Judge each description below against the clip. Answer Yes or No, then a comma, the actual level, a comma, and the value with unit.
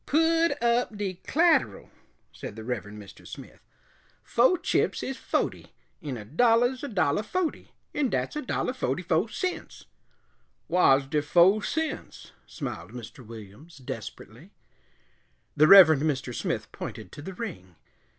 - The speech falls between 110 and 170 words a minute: Yes, average, 140 wpm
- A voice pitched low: No, medium, 180 Hz